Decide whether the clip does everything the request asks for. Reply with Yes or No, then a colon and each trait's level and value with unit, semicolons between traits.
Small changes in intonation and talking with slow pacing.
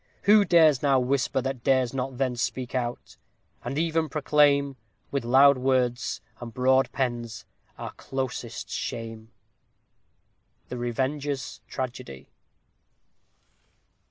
Yes: narrow, 2.3 semitones; slow, 105 wpm